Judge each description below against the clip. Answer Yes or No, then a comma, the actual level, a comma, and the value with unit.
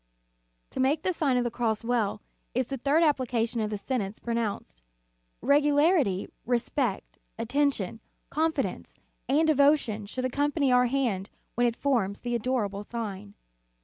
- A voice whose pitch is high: Yes, high, 245 Hz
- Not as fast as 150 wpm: Yes, average, 140 wpm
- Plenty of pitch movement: No, average, 4.6 semitones